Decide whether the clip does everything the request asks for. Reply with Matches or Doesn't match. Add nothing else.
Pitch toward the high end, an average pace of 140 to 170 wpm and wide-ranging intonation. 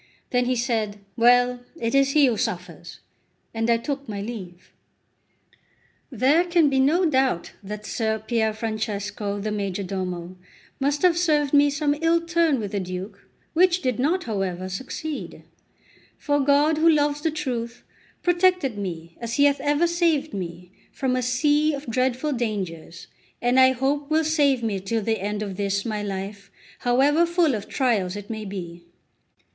Matches